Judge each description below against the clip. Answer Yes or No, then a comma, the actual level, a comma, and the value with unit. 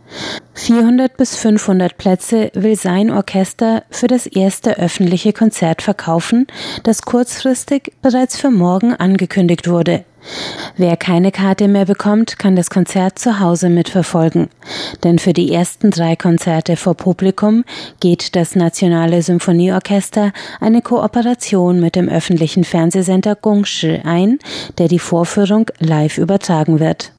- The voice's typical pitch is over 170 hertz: Yes, high, 190 Hz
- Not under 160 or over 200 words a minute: No, slow, 125 wpm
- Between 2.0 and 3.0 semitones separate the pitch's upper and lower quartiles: No, average, 3.9 semitones